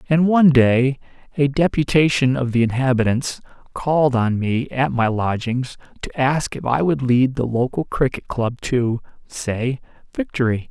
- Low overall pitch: Yes, low, 130 Hz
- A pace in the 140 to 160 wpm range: Yes, average, 150 wpm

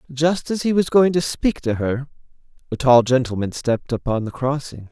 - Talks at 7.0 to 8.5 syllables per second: No, 5.2 syllables/s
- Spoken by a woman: No, male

